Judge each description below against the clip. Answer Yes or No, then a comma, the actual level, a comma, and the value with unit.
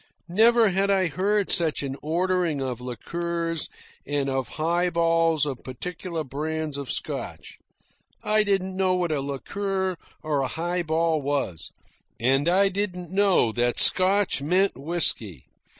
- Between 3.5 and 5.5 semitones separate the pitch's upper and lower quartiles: Yes, average, 4.7 semitones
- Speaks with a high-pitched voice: No, medium, 165 Hz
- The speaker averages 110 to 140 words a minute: Yes, slow, 135 wpm